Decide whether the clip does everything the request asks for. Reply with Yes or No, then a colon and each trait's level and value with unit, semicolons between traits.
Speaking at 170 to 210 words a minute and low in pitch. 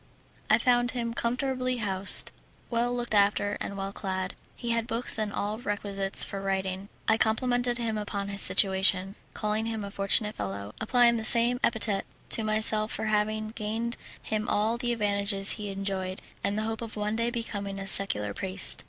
No: average, 180 wpm; high, 215 Hz